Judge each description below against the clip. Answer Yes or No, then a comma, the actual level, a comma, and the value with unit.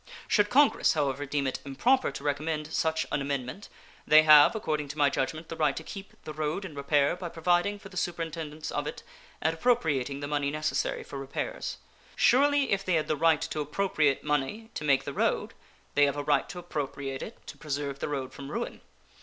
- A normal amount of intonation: Yes, average, 3.6 semitones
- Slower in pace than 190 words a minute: No, fast, 205 wpm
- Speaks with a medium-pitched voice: Yes, medium, 150 Hz